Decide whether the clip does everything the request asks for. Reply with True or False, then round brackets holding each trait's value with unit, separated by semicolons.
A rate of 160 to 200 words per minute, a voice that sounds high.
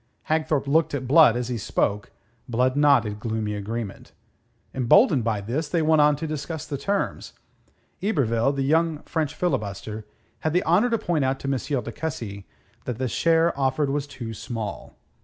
False (170 wpm; 140 Hz)